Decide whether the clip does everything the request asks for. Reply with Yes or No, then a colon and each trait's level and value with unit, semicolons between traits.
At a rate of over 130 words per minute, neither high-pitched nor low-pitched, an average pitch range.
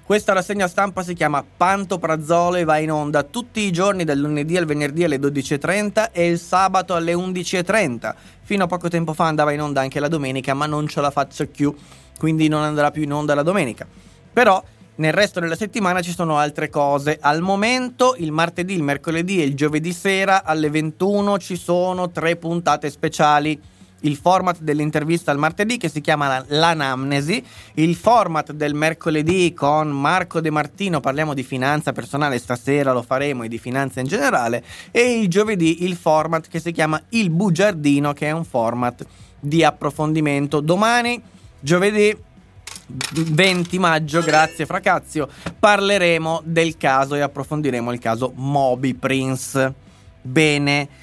Yes: average, 160 wpm; medium, 155 Hz; average, 3.8 semitones